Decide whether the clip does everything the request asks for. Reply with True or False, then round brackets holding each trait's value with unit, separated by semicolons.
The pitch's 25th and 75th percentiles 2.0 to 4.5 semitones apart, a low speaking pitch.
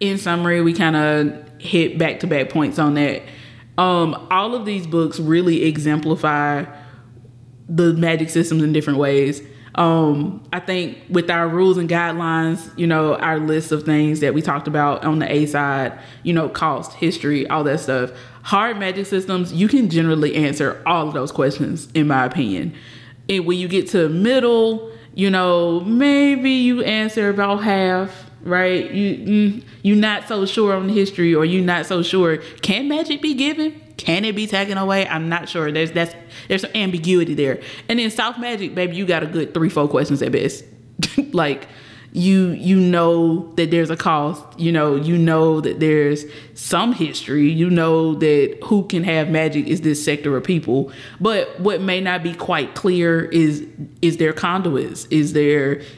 False (3.9 semitones; 165 Hz)